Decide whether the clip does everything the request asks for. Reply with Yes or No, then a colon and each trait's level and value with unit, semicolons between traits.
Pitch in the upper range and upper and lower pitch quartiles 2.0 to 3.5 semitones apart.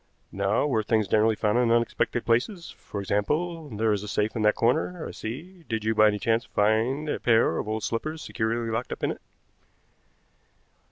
No: low, 115 Hz; average, 3.0 semitones